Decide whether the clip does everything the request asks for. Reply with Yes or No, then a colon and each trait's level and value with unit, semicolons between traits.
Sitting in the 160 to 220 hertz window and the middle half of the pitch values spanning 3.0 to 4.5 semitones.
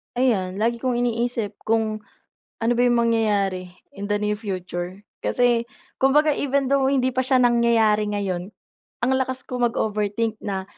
No: high, 230 Hz; average, 3.3 semitones